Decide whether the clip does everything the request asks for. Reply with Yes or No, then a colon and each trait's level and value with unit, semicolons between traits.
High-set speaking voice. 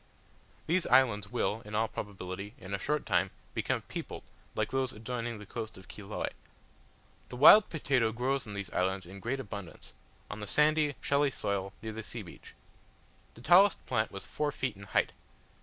No: low, 110 Hz